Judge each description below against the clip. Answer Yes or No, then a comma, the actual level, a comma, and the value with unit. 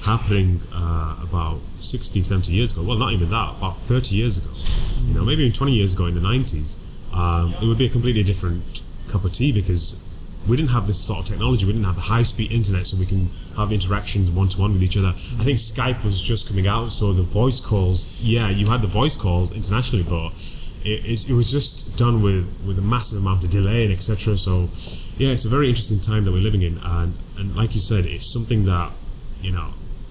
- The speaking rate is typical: No, fast, 225 wpm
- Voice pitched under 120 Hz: Yes, low, 100 Hz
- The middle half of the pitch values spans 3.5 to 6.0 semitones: Yes, average, 4.0 semitones